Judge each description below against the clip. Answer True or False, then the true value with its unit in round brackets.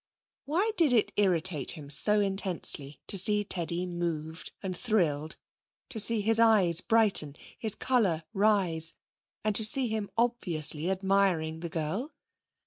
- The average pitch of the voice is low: False (195 Hz)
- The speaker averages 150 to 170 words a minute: False (135 wpm)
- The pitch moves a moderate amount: True (5.0 semitones)